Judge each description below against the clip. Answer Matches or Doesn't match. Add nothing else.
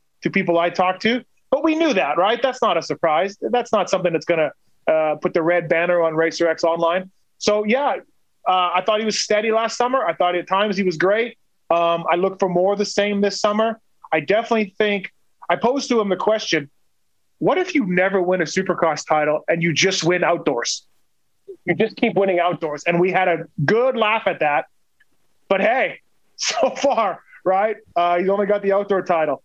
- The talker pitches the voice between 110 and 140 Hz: Doesn't match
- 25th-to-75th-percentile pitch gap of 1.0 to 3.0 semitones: Doesn't match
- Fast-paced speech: Matches